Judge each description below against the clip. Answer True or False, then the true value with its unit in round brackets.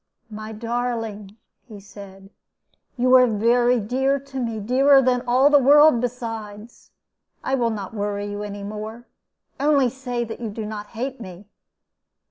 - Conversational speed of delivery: True (150 wpm)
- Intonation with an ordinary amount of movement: True (3.3 semitones)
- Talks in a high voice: True (230 Hz)